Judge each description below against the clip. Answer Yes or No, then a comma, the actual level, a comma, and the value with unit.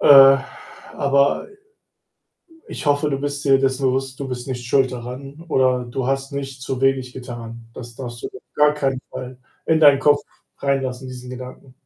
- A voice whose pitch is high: No, low, 135 Hz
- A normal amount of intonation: No, narrow, 1.6 semitones